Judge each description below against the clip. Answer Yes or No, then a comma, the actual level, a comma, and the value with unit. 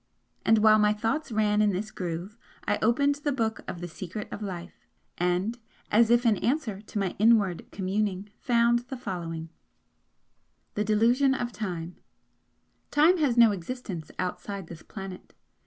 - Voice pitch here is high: Yes, high, 210 Hz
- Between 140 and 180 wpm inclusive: Yes, average, 155 wpm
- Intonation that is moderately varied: Yes, average, 4.2 semitones